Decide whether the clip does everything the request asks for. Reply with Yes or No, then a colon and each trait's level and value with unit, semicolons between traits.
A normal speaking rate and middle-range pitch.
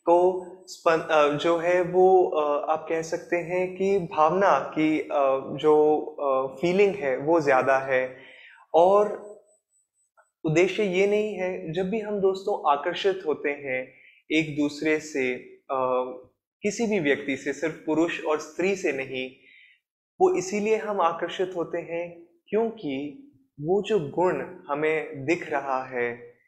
Yes: average, 130 wpm; medium, 165 Hz